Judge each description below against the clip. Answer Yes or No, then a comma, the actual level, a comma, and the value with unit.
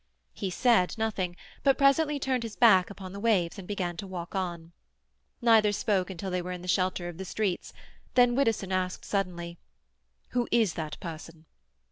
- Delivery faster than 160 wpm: Yes, average, 175 wpm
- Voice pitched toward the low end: No, high, 190 Hz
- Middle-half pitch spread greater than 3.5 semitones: Yes, average, 3.9 semitones